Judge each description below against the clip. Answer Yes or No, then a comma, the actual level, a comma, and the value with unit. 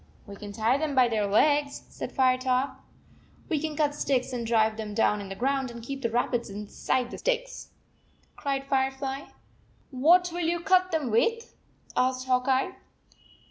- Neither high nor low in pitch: No, very high, 265 Hz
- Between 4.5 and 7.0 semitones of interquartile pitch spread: No, average, 3.9 semitones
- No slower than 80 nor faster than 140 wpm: No, average, 170 wpm